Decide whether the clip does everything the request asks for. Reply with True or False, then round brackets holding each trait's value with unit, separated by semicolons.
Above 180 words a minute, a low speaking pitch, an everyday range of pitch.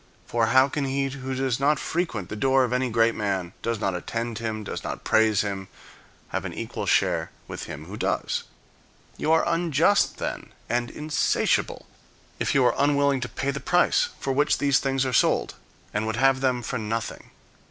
True (190 wpm; 130 Hz; 3.9 semitones)